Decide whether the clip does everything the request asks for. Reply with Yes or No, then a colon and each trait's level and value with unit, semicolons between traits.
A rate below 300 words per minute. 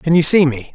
No: fast, 325 wpm